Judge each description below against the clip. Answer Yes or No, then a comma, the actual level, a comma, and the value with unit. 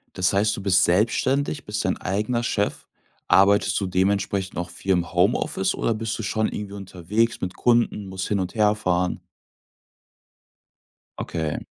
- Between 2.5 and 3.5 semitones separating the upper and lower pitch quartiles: Yes, average, 2.8 semitones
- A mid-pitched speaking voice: No, low, 100 Hz